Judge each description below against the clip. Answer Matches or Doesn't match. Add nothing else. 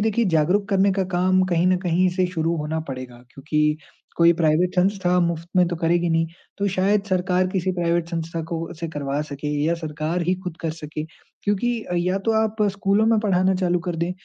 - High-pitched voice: Doesn't match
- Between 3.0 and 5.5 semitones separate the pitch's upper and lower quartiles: Doesn't match